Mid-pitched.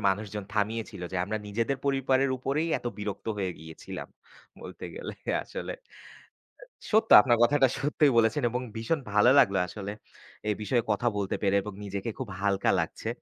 No: low, 115 Hz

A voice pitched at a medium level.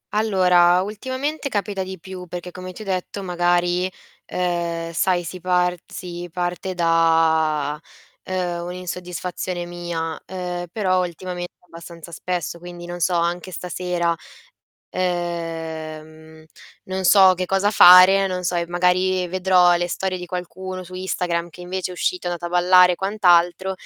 Yes: medium, 180 Hz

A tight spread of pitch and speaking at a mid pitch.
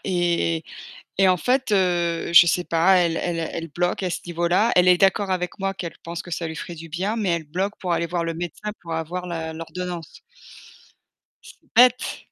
Yes: narrow, 1.9 semitones; medium, 175 Hz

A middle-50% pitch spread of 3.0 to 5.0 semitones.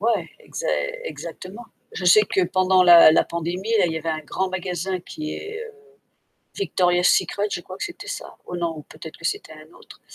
No: narrow, 2.6 semitones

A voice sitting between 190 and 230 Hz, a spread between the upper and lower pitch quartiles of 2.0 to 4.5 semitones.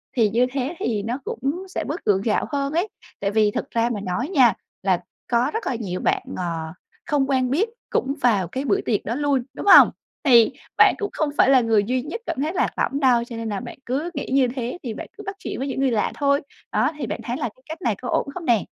No: very high, 255 Hz; average, 3.9 semitones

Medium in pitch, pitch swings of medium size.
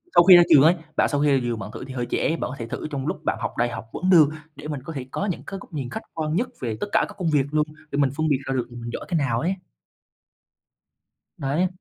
Yes: medium, 145 Hz; average, 4.5 semitones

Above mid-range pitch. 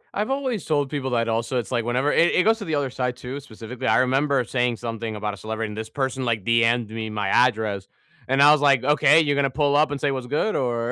No: low, 125 Hz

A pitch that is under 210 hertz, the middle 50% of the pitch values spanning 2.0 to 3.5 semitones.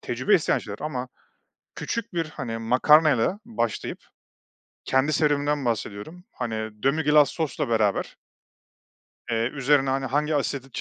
No: medium, 140 Hz; average, 4.0 semitones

